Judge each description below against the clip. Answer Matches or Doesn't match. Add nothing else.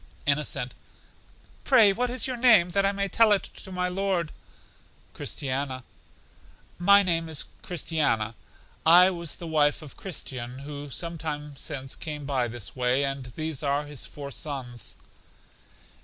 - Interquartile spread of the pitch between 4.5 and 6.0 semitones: Matches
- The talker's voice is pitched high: Doesn't match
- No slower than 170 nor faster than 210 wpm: Doesn't match